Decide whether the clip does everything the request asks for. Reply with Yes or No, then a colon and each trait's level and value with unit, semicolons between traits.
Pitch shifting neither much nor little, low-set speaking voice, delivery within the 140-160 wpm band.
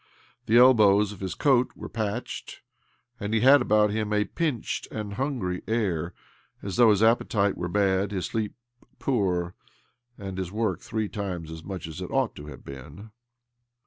No: average, 3.2 semitones; low, 105 Hz; average, 170 wpm